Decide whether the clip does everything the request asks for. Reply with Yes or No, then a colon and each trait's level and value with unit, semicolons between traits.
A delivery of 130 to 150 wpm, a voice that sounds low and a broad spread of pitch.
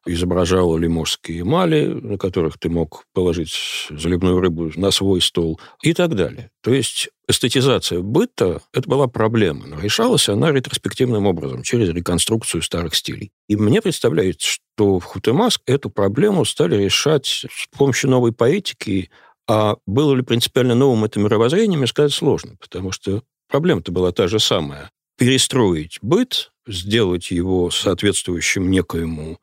Yes: average, 140 wpm; low, 100 Hz; wide, 6.3 semitones